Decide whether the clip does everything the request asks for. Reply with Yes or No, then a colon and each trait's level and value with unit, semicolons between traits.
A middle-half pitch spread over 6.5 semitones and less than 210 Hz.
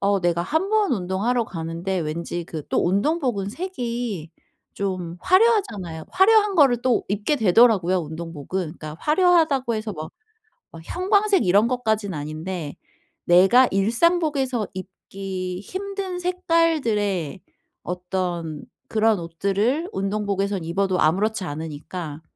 Yes: wide, 7.4 semitones; high, 200 Hz